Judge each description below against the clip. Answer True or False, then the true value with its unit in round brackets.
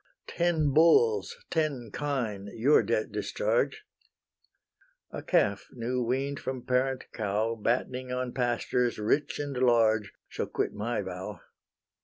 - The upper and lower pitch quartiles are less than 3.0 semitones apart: False (4.0 semitones)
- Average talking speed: False (120 wpm)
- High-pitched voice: False (125 Hz)